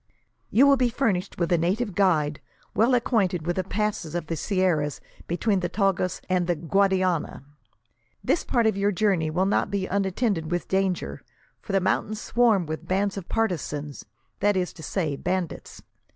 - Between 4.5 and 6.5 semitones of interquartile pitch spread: No, average, 3.1 semitones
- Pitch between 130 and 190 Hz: Yes, medium, 185 Hz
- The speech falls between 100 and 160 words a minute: No, average, 170 wpm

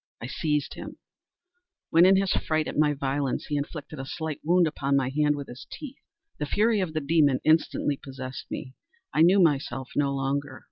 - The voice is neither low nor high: Yes, medium, 150 Hz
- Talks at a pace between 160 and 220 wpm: Yes, average, 190 wpm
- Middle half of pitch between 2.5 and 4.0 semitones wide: Yes, average, 2.8 semitones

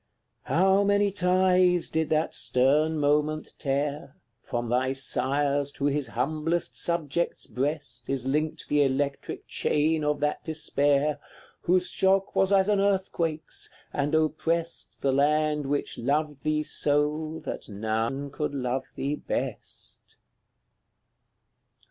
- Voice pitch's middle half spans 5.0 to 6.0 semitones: No, narrow, 2.6 semitones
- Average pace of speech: No, slow, 120 wpm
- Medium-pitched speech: Yes, medium, 150 Hz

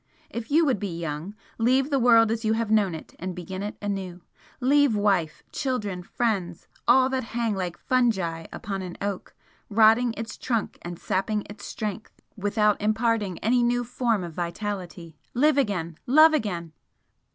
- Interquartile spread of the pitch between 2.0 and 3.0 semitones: No, average, 4.6 semitones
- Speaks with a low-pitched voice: No, high, 210 Hz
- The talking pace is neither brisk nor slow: Yes, average, 165 wpm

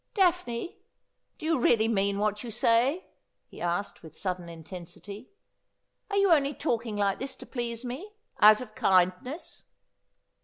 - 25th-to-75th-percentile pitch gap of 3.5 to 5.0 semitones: No, wide, 5.6 semitones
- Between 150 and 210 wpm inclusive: Yes, average, 165 wpm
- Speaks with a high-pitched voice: Yes, high, 225 Hz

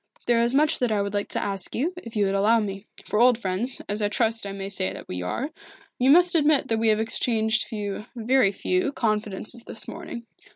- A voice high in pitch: Yes, high, 220 Hz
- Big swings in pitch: No, average, 3.5 semitones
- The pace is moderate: No, fast, 225 wpm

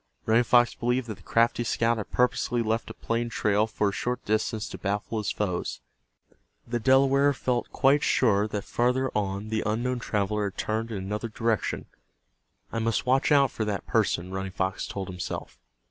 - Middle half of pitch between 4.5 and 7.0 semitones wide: No, average, 2.9 semitones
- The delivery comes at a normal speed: Yes, average, 180 wpm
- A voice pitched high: No, low, 110 Hz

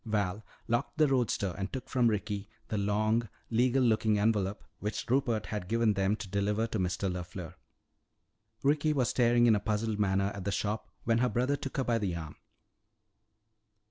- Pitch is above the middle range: No, low, 110 Hz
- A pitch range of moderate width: Yes, average, 3.0 semitones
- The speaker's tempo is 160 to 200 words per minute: Yes, average, 175 wpm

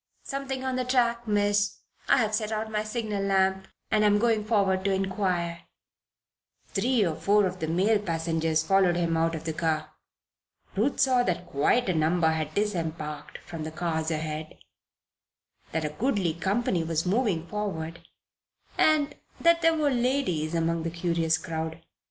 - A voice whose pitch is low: No, high, 190 Hz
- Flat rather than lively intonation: No, average, 4.9 semitones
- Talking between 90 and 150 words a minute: No, average, 160 wpm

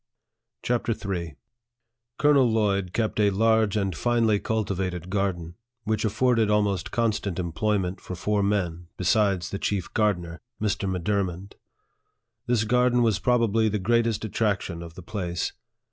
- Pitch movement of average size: Yes, average, 3.3 semitones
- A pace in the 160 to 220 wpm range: No, average, 140 wpm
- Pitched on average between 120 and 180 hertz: No, low, 105 Hz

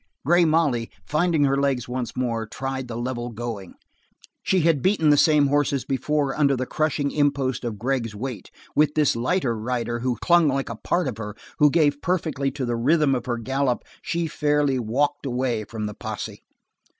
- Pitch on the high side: No, low, 135 Hz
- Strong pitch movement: No, average, 3.7 semitones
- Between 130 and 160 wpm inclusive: No, average, 185 wpm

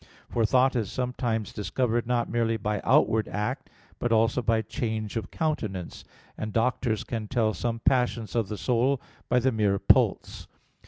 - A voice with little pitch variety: Yes, narrow, 2.2 semitones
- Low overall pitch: Yes, low, 115 Hz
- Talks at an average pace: Yes, average, 160 wpm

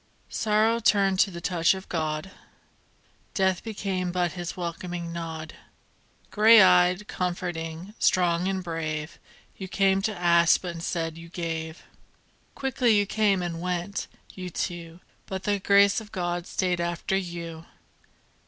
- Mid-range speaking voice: Yes, medium, 180 Hz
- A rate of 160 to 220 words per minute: No, slow, 135 wpm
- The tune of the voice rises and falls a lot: No, narrow, 2.4 semitones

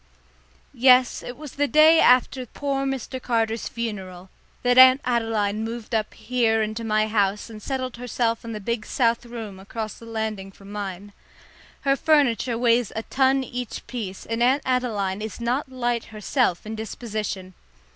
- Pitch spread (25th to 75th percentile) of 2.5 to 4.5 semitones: Yes, average, 2.9 semitones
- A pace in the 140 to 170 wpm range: Yes, average, 160 wpm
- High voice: Yes, high, 230 Hz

